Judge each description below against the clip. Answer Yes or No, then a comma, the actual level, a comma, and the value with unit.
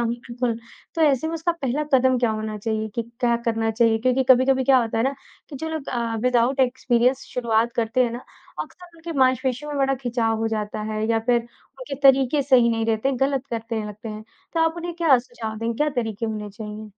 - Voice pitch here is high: Yes, high, 245 Hz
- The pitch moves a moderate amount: Yes, average, 3.1 semitones